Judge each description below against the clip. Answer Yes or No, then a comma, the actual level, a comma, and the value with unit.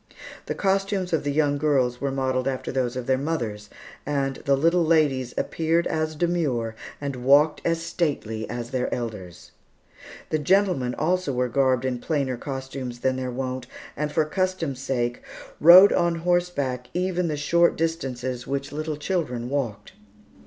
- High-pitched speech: No, medium, 140 Hz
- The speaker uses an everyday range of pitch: Yes, average, 4.6 semitones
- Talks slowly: No, average, 155 wpm